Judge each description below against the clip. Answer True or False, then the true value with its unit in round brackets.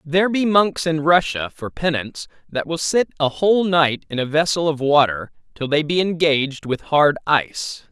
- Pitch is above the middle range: False (155 Hz)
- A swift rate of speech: False (190 wpm)